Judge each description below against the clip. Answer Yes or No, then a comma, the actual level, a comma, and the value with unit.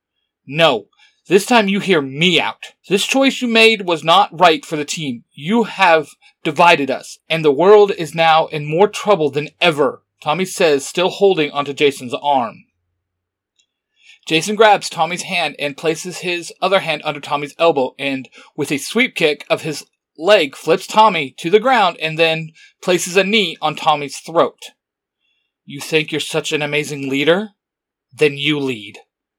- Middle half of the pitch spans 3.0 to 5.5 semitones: Yes, average, 4.6 semitones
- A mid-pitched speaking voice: Yes, medium, 160 Hz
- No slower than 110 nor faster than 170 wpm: Yes, average, 165 wpm